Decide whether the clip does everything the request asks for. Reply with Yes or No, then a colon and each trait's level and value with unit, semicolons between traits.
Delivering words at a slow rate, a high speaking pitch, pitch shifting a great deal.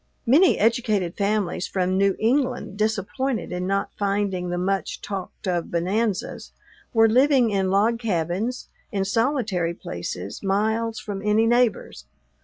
No: slow, 130 wpm; high, 205 Hz; average, 3.4 semitones